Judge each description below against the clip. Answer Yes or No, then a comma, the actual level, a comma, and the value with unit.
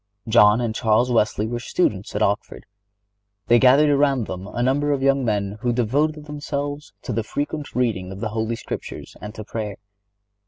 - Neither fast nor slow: Yes, average, 180 wpm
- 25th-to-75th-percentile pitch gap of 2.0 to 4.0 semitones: No, average, 4.8 semitones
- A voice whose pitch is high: No, low, 120 Hz